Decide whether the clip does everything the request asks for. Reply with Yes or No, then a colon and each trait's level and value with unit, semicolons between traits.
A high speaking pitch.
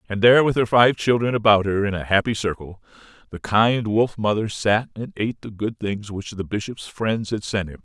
No: low, 105 Hz